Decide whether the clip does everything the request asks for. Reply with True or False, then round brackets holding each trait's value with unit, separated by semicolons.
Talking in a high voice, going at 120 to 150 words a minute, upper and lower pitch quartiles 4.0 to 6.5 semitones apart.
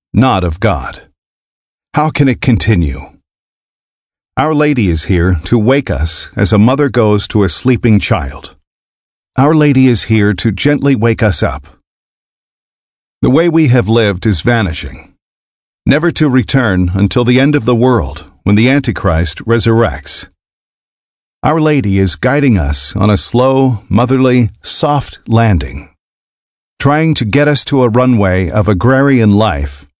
False (115 Hz; 145 wpm; 5.6 semitones)